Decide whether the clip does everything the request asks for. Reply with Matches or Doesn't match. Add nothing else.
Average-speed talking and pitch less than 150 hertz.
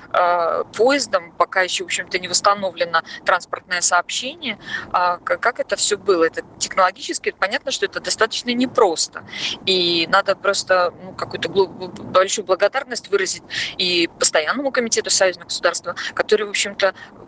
Doesn't match